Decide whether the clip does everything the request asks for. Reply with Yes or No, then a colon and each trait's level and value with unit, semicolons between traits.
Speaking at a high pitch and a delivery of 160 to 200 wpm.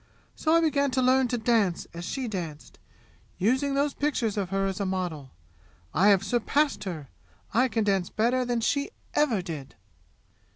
Yes: high, 220 Hz; average, 170 wpm